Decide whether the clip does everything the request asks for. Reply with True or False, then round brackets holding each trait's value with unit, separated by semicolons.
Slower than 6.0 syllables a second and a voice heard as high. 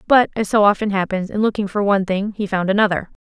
False (6.5 syllables/s; 200 Hz)